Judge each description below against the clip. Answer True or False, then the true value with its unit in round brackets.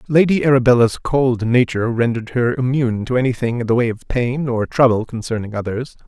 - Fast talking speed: False (180 wpm)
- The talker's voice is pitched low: True (120 Hz)